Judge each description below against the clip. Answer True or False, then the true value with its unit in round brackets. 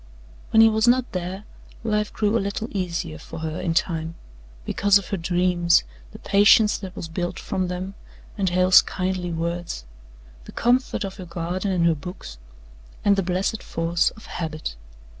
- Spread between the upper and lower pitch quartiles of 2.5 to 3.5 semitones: True (2.9 semitones)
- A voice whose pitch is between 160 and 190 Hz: True (185 Hz)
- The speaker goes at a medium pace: True (170 wpm)